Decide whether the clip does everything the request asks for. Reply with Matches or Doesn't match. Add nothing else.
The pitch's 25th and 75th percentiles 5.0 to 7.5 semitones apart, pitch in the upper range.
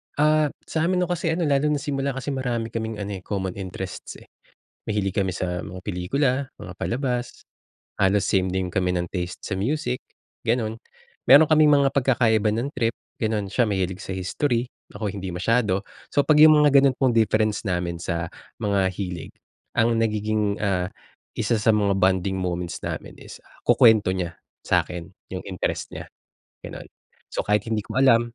Doesn't match